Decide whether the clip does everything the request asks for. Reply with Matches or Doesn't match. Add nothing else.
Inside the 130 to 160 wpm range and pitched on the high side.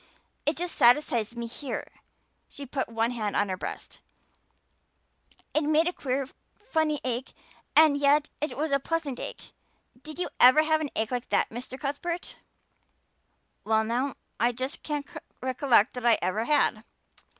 Matches